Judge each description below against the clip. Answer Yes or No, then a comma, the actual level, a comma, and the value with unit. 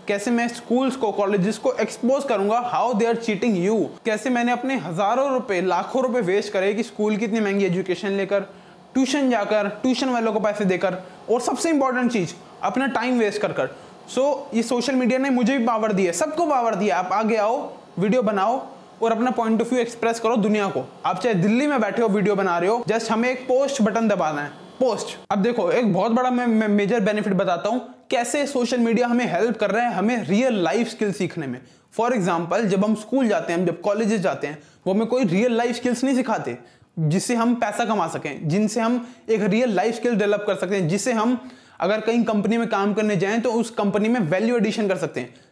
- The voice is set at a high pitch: Yes, high, 220 Hz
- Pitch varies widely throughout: No, average, 3.6 semitones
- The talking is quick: No, average, 170 wpm